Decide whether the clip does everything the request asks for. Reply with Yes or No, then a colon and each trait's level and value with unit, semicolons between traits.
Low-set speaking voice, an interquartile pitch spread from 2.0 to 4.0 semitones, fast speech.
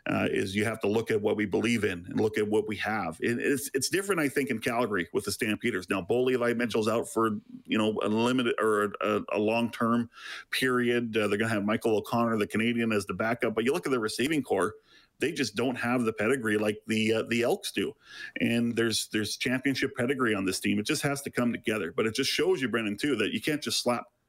Yes: low, 115 Hz; narrow, 2.4 semitones; fast, 245 wpm